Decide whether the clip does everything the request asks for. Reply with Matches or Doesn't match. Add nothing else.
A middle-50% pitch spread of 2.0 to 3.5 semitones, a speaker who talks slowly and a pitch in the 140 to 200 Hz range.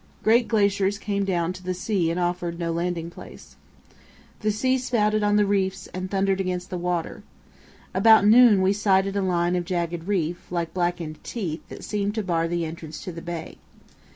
Doesn't match